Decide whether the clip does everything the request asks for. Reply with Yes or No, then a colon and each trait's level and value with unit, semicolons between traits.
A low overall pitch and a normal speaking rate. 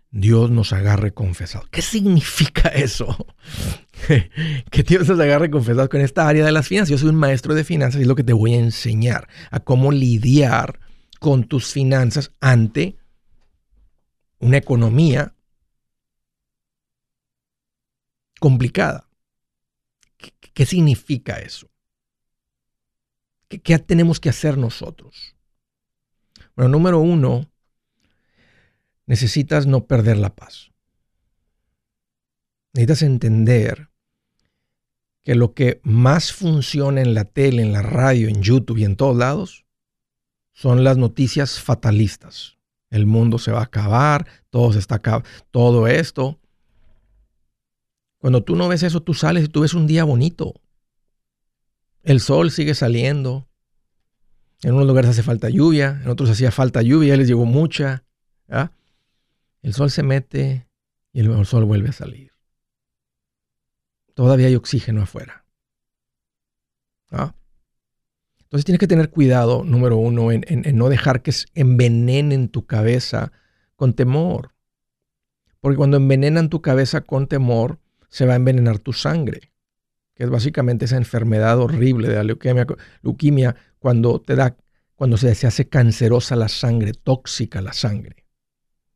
Yes: low, 130 Hz; average, 135 wpm